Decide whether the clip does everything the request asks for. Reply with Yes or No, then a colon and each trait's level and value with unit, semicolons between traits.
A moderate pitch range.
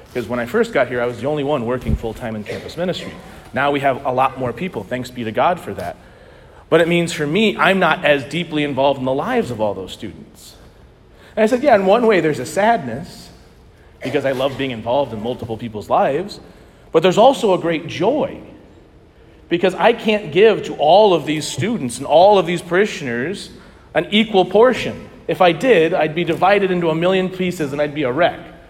No: wide, 6.9 semitones